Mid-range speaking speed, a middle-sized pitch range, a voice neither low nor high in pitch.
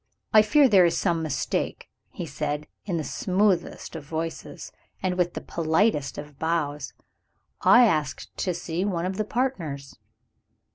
Yes: average, 150 wpm; average, 4.3 semitones; medium, 170 Hz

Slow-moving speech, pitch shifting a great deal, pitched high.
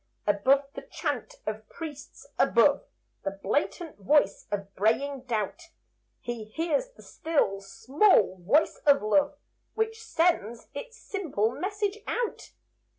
Yes: slow, 120 wpm; wide, 8.6 semitones; very high, 280 Hz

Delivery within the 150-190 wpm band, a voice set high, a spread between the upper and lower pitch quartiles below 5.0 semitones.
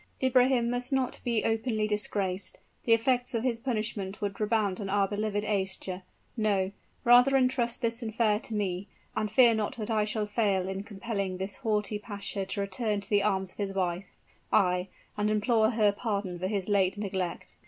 Yes: average, 180 wpm; high, 210 Hz; average, 2.7 semitones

